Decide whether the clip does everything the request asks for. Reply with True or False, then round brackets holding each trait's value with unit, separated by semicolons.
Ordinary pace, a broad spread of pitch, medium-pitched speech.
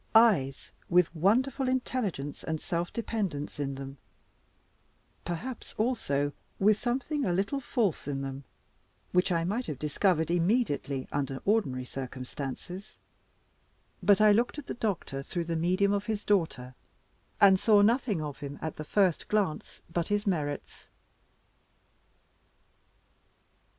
False (130 wpm; 6.7 semitones; 180 Hz)